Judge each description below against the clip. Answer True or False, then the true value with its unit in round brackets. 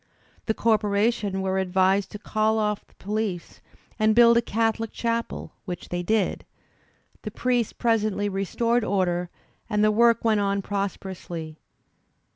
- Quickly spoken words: False (140 wpm)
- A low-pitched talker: False (210 Hz)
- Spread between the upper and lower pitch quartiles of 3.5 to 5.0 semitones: False (2.8 semitones)